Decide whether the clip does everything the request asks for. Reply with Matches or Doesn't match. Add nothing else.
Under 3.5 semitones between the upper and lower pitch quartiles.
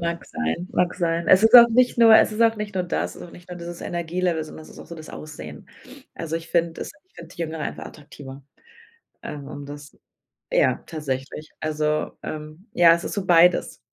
Matches